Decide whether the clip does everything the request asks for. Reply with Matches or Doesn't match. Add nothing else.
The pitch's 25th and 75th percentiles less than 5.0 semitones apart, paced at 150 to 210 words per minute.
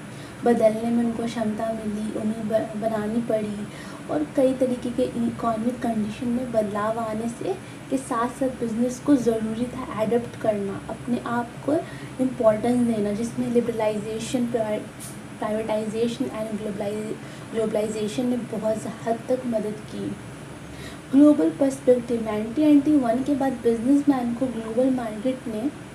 Doesn't match